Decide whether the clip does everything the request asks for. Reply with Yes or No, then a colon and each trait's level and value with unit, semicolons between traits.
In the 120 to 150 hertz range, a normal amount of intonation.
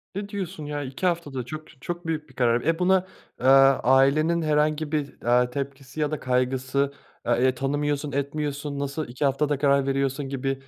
No: medium, 140 Hz; narrow, 2.3 semitones